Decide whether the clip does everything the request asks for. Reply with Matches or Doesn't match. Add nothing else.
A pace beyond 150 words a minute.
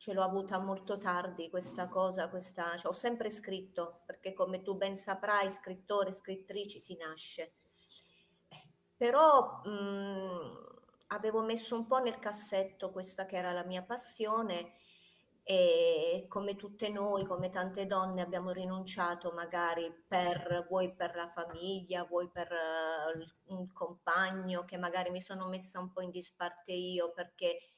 Doesn't match